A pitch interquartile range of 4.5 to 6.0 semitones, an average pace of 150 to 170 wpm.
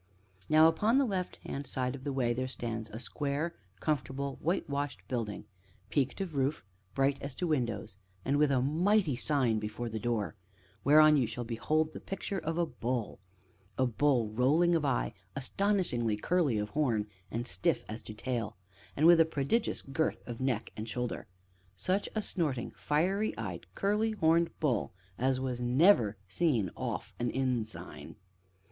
Yes: average, 5.3 semitones; average, 165 wpm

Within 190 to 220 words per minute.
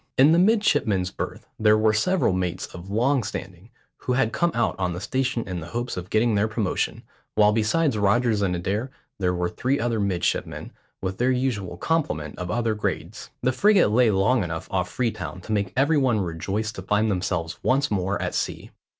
Yes: average, 195 wpm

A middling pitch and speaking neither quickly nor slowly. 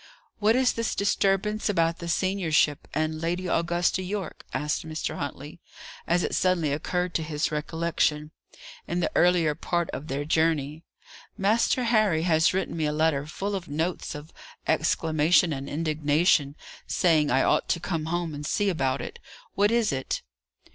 Yes: medium, 165 Hz; average, 160 wpm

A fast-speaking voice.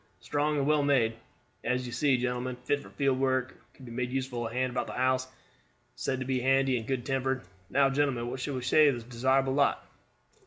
Yes: fast, 225 wpm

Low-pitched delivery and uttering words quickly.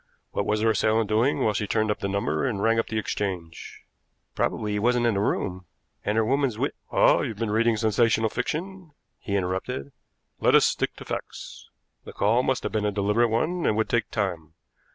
Yes: low, 110 Hz; fast, 210 wpm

